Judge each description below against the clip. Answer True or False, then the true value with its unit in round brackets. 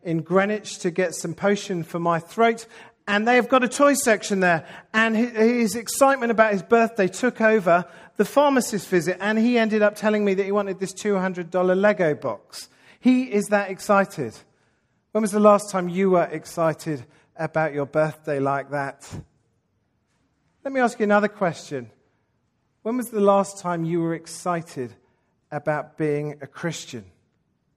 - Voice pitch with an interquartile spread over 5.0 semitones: True (5.4 semitones)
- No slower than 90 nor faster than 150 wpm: False (160 wpm)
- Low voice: False (185 Hz)